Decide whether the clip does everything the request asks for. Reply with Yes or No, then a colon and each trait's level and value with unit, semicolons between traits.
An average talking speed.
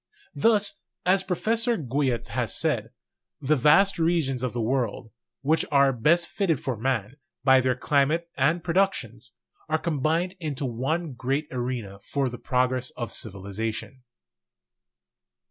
No: slow, 130 wpm